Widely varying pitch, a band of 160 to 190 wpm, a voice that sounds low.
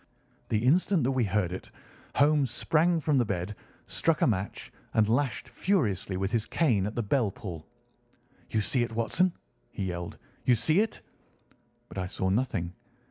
Yes: wide, 6.6 semitones; average, 170 wpm; low, 115 Hz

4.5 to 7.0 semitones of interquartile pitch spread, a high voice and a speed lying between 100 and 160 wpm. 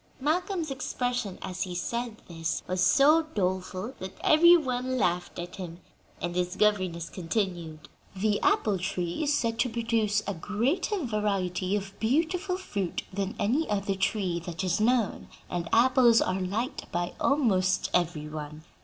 Yes: wide, 5.4 semitones; high, 200 Hz; average, 150 wpm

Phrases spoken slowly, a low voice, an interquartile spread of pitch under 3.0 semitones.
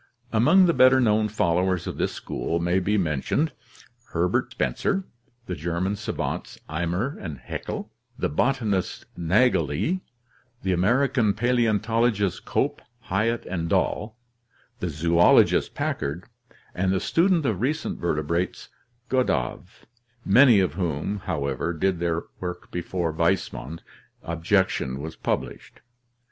No: slow, 120 wpm; very low, 95 Hz; wide, 5.5 semitones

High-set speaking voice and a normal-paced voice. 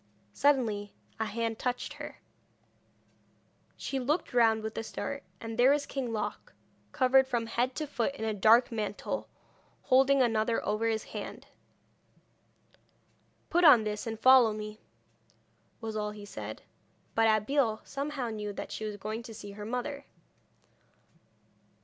Yes: high, 225 Hz; average, 145 wpm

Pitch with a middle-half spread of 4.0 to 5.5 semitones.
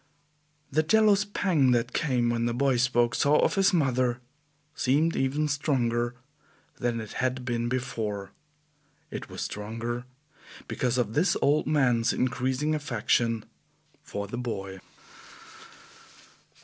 No: average, 3.6 semitones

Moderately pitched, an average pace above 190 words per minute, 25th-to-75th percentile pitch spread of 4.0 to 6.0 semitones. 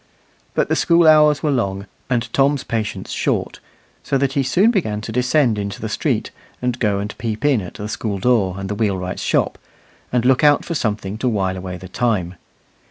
No: low, 115 Hz; average, 200 wpm; average, 5.3 semitones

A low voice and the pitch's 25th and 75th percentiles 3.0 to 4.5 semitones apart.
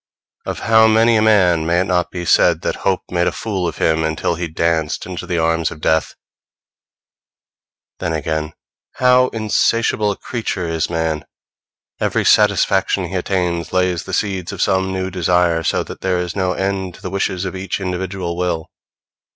No: very low, 90 Hz; narrow, 2.5 semitones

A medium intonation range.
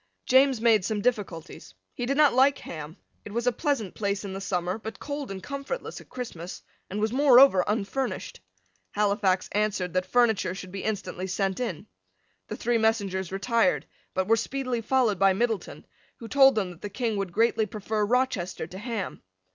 Yes: average, 4.4 semitones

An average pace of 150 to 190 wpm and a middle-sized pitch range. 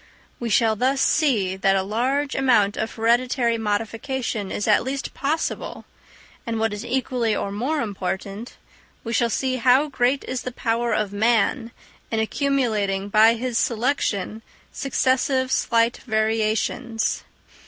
No: slow, 135 wpm; average, 3.1 semitones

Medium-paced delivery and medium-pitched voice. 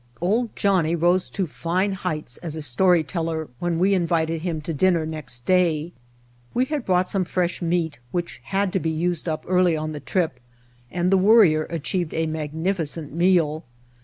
Yes: average, 175 wpm; medium, 170 Hz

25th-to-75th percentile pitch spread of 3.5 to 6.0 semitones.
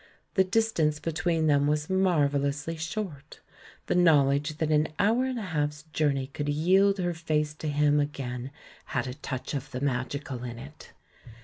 No: average, 2.7 semitones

